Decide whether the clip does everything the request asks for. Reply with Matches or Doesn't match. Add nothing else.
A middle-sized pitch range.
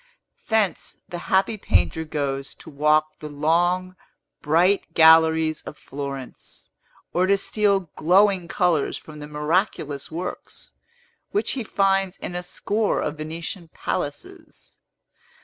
Matches